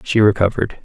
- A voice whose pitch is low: Yes, low, 105 Hz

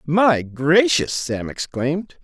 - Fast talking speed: No, slow, 105 wpm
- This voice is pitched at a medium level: Yes, medium, 160 Hz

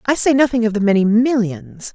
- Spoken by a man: No, female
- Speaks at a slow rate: No, fast, 215 wpm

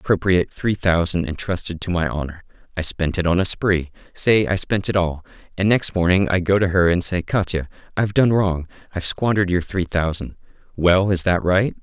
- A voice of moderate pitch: No, very low, 90 Hz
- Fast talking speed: Yes, fast, 210 wpm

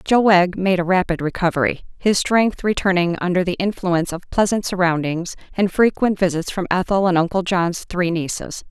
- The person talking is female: Yes, female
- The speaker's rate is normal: Yes, average, 170 wpm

